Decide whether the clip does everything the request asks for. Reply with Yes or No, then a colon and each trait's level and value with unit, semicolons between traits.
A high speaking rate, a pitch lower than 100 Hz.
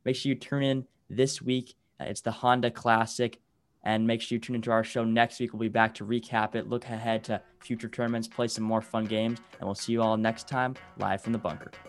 No: fast, 240 wpm; low, 115 Hz